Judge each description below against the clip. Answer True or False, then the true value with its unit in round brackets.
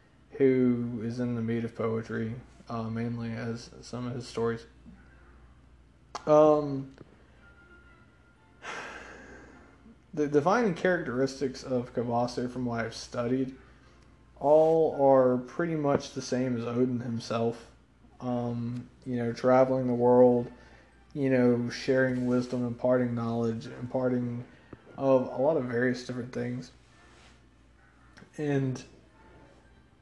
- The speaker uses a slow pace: True (110 wpm)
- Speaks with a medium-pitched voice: False (125 Hz)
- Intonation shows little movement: True (2.1 semitones)